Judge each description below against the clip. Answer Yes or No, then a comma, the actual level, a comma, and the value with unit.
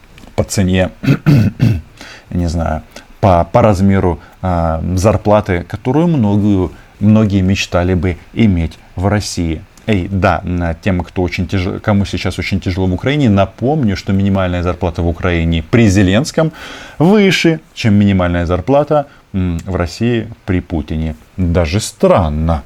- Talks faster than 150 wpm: No, average, 125 wpm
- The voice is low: Yes, very low, 95 Hz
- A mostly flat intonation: No, average, 3.4 semitones